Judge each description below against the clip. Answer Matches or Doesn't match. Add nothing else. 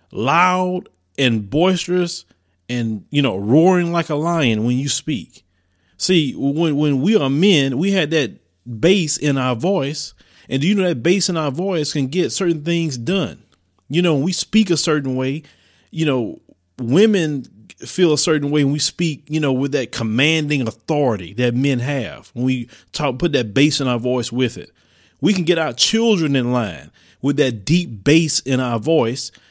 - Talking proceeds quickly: Doesn't match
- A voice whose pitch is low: Doesn't match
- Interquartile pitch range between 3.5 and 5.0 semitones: Doesn't match